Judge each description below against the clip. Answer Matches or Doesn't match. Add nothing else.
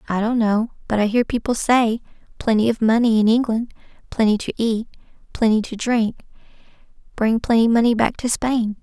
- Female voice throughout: Matches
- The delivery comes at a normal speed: Matches